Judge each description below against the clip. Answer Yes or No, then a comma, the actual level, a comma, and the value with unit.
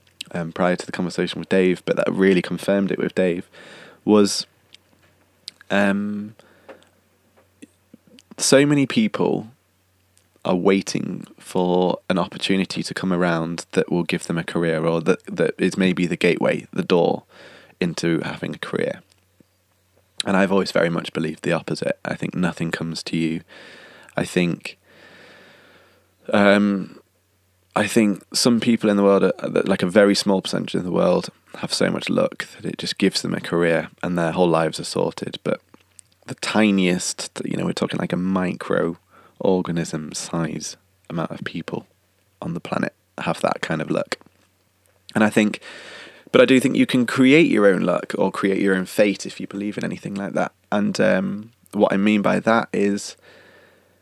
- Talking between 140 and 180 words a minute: Yes, average, 170 wpm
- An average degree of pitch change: No, narrow, 2.3 semitones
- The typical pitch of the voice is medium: No, very low, 95 Hz